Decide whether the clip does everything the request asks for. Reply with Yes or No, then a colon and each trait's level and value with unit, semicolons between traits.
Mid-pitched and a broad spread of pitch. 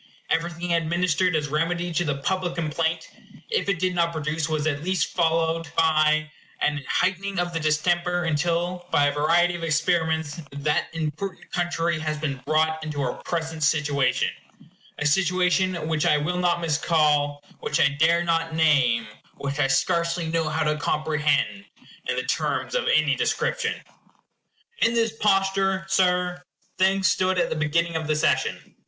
No: medium, 165 Hz; narrow, 2.6 semitones